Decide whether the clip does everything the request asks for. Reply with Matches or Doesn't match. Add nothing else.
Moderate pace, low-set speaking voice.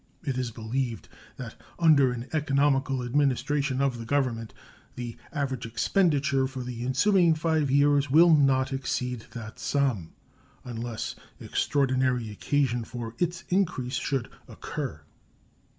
Doesn't match